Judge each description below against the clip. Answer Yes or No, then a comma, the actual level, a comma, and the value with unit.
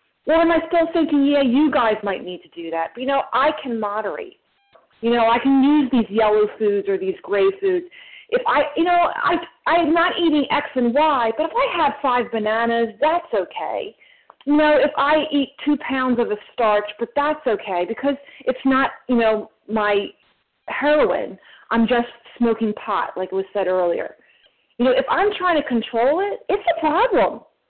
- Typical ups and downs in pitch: No, wide, 6.1 semitones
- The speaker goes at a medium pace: Yes, average, 195 wpm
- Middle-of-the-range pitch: No, very high, 270 Hz